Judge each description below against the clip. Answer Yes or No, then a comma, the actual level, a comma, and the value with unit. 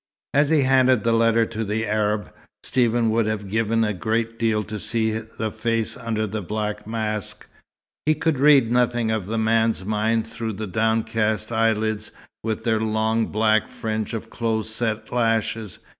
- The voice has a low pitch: Yes, low, 110 Hz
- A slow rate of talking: No, average, 165 wpm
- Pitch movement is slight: Yes, narrow, 1.0 semitones